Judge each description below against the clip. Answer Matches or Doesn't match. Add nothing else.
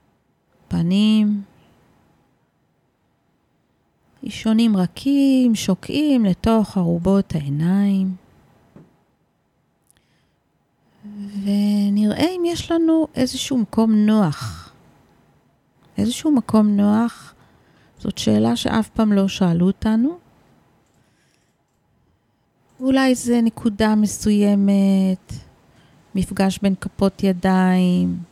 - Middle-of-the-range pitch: Doesn't match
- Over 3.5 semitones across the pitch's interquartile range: Doesn't match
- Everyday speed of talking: Doesn't match